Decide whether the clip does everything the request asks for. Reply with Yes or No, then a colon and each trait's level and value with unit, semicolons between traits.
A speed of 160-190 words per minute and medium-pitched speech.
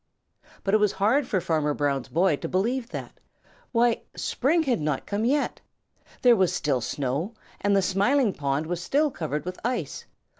No: average, 175 wpm; high, 195 Hz